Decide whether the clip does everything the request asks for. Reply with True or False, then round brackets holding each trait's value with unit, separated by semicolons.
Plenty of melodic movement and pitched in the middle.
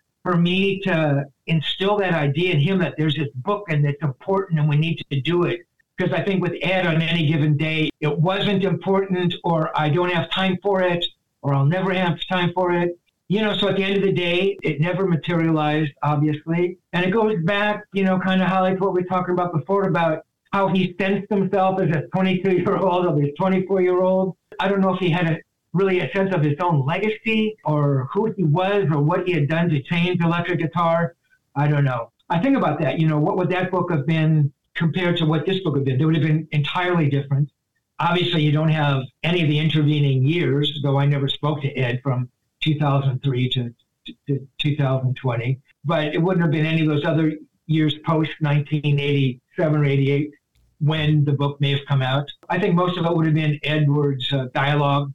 False (3.8 semitones; 165 Hz)